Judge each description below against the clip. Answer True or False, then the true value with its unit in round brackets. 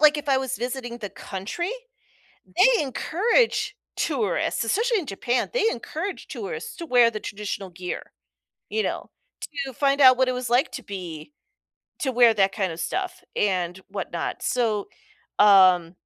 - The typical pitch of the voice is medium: False (245 Hz)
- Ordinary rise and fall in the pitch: False (7.4 semitones)